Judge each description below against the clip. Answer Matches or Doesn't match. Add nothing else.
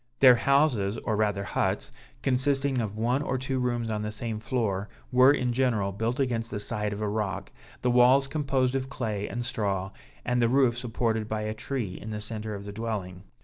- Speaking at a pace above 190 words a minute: Matches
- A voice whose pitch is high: Doesn't match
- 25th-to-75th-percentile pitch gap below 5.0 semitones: Matches